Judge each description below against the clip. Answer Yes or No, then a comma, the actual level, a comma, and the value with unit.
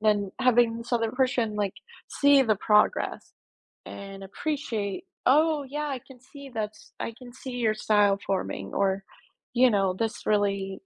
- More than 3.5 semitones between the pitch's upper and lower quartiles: Yes, average, 4.2 semitones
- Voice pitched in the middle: No, high, 225 Hz